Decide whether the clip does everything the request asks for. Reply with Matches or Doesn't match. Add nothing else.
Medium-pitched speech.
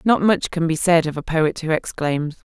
Matches